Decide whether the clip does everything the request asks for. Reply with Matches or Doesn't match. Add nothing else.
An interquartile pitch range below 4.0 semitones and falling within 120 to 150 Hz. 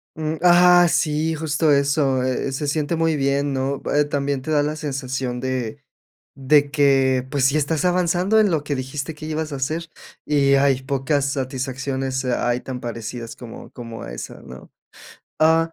Matches